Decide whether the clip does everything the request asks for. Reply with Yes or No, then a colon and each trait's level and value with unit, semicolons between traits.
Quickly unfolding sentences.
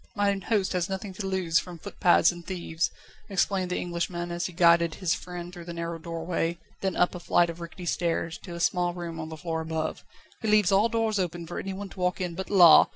Yes: fast, 225 wpm